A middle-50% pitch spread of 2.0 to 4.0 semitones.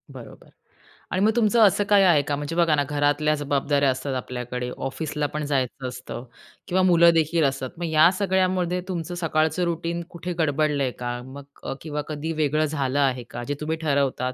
Yes: average, 3.6 semitones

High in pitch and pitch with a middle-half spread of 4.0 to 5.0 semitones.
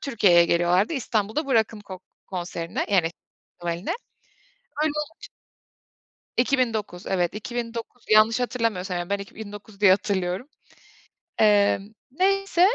Yes: high, 210 Hz; average, 4.7 semitones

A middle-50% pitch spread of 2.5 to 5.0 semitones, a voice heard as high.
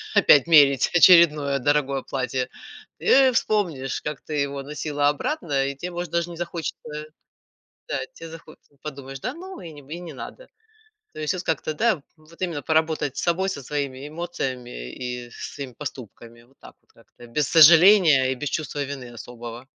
No: average, 3.9 semitones; medium, 150 Hz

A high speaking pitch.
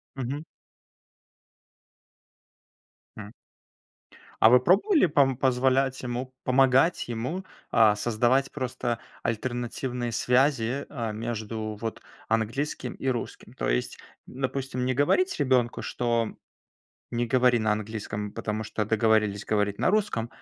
No: low, 120 Hz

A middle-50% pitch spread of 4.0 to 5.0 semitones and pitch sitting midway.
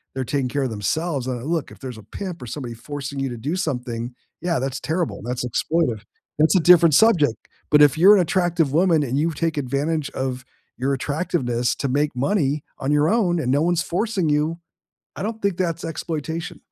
Yes: average, 4.5 semitones; medium, 150 Hz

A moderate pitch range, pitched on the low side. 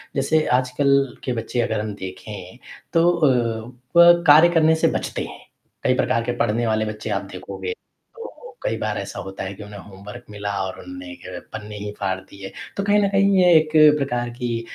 No: wide, 8.0 semitones; low, 120 Hz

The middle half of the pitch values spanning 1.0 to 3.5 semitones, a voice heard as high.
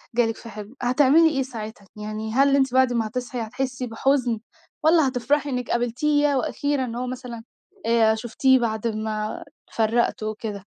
Yes: average, 3.2 semitones; high, 245 Hz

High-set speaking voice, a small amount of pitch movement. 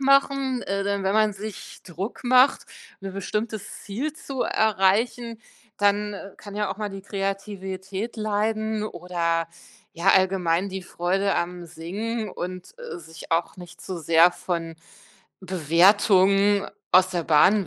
No: high, 195 Hz; average, 3.1 semitones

